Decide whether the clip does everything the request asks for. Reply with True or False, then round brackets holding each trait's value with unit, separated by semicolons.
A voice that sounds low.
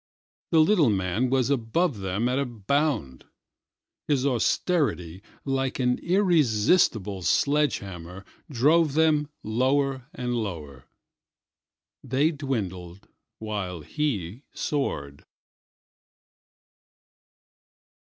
True (125 Hz)